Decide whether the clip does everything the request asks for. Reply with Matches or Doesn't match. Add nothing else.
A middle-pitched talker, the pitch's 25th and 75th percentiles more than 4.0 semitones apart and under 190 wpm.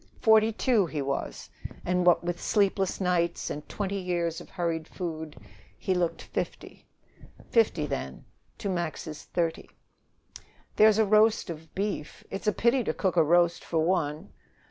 Doesn't match